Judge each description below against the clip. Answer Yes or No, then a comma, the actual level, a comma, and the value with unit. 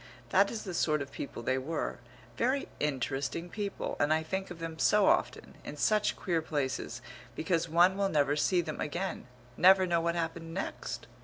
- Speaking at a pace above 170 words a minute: Yes, average, 180 wpm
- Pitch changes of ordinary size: Yes, average, 4.1 semitones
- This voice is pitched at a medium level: Yes, medium, 165 Hz